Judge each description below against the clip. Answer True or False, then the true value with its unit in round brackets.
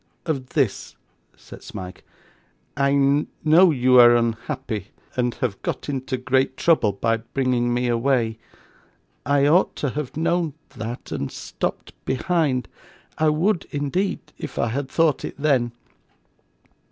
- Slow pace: True (130 wpm)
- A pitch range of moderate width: True (3.9 semitones)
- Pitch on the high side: False (130 Hz)